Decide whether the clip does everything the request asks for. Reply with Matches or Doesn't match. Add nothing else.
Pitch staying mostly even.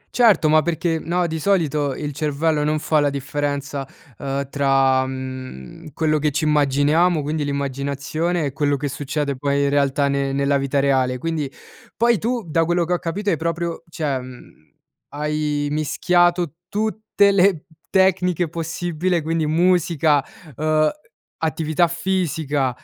Doesn't match